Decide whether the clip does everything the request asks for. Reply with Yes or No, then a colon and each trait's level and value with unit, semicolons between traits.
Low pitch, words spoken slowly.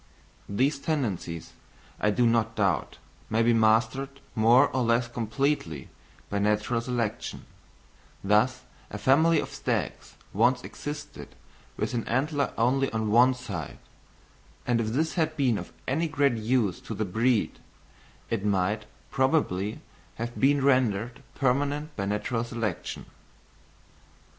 Yes: low, 120 Hz; slow, 130 wpm